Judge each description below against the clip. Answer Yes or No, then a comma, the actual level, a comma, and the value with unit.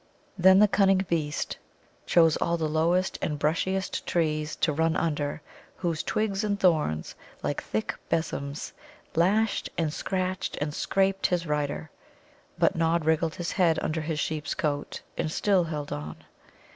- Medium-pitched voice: Yes, medium, 165 Hz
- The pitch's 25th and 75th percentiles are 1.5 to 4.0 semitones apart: Yes, average, 3.5 semitones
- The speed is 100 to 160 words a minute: Yes, average, 145 wpm